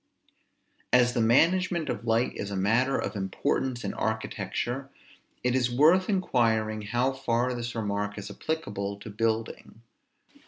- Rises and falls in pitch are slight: No, average, 3.4 semitones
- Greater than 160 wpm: No, slow, 135 wpm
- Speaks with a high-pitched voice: No, low, 120 Hz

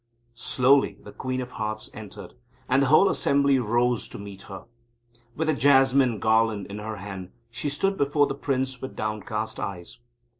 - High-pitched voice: No, low, 120 Hz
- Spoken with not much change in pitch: No, average, 4.3 semitones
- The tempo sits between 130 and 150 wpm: No, average, 165 wpm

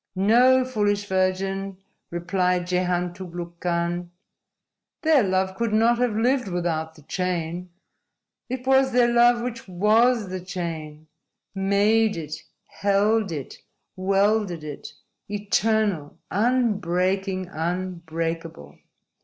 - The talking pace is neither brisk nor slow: No, slow, 105 wpm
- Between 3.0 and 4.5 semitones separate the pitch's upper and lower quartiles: Yes, average, 4.0 semitones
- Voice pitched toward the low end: No, high, 190 Hz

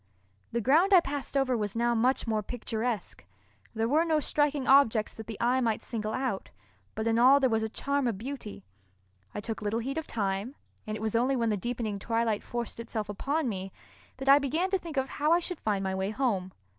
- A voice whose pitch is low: No, high, 235 Hz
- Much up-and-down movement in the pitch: No, average, 4.1 semitones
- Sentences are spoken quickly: Yes, fast, 220 wpm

